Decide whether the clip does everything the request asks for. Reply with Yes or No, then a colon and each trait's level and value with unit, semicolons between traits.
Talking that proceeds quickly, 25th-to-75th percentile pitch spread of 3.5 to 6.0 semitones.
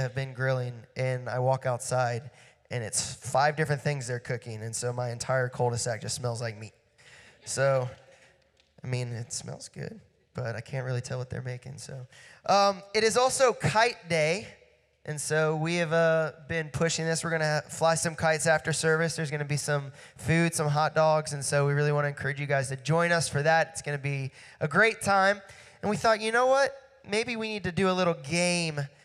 Yes: fast, 210 wpm; average, 4.4 semitones